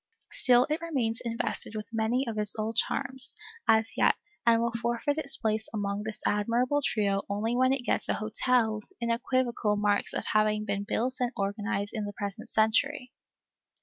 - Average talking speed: Yes, average, 175 wpm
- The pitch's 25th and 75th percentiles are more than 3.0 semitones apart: No, average, 2.7 semitones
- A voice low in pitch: No, high, 225 Hz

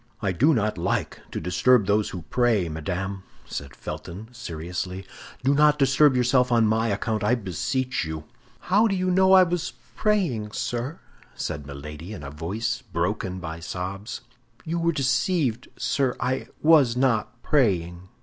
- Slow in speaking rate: No, average, 155 wpm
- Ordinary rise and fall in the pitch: No, wide, 6.8 semitones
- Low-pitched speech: Yes, low, 115 Hz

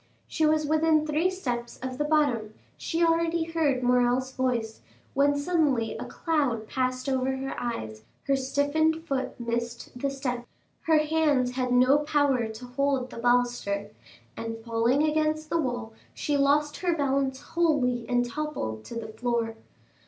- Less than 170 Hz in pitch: No, very high, 265 Hz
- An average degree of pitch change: Yes, average, 3.9 semitones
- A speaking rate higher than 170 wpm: No, average, 150 wpm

